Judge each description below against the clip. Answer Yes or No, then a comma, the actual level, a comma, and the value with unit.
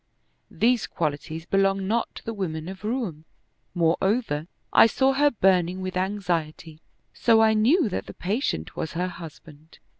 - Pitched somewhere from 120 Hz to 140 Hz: No, high, 190 Hz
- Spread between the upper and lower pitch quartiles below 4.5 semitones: No, average, 5.3 semitones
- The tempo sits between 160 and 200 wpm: No, average, 150 wpm